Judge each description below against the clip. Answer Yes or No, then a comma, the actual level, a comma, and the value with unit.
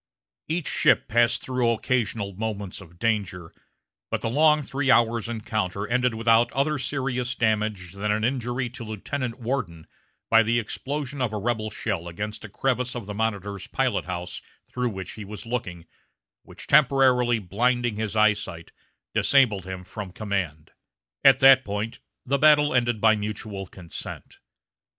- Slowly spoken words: No, average, 155 wpm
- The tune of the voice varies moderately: Yes, average, 3.8 semitones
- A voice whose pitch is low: Yes, low, 110 Hz